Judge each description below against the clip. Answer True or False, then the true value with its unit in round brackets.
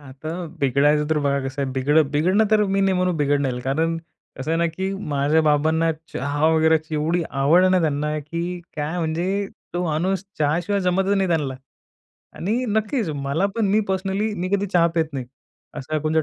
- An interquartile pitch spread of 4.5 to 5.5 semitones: False (3.9 semitones)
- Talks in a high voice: False (160 Hz)